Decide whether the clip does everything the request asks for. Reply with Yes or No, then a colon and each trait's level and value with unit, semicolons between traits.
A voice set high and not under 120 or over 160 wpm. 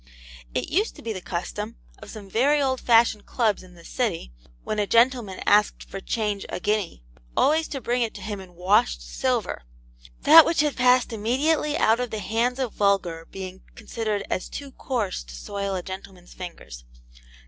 No: high, 210 Hz; average, 180 wpm